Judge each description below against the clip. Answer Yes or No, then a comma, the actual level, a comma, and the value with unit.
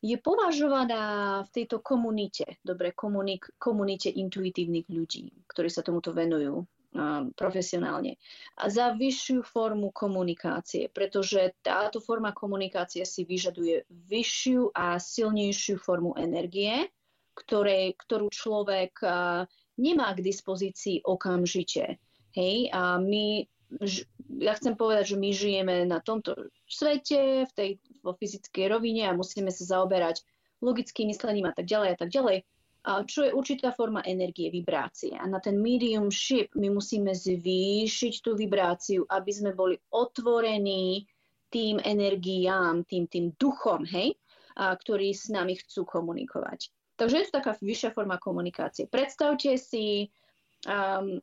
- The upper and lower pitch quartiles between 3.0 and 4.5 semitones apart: Yes, average, 3.9 semitones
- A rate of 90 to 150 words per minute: Yes, average, 130 wpm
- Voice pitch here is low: No, high, 200 Hz